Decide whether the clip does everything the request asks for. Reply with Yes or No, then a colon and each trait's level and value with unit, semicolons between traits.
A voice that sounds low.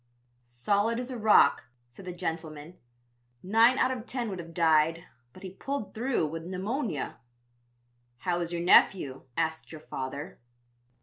No: medium, 175 Hz